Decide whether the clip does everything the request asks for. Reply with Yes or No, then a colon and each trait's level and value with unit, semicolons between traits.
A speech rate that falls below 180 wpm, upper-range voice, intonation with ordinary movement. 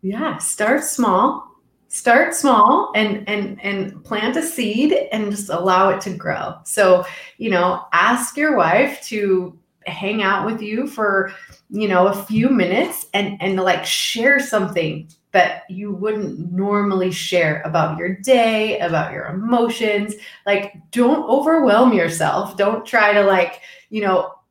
Yes: average, 145 wpm; high, 205 Hz; average, 3.9 semitones